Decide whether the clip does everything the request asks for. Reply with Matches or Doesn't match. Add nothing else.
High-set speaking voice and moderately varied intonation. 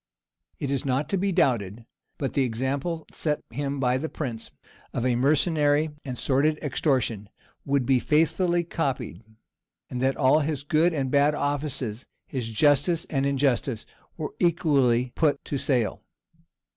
Doesn't match